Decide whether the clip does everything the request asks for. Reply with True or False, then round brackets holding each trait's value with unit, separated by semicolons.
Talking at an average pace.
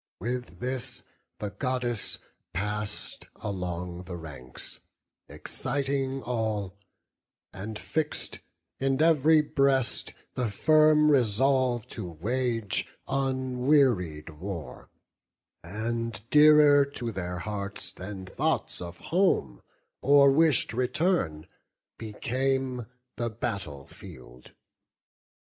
False (90 wpm)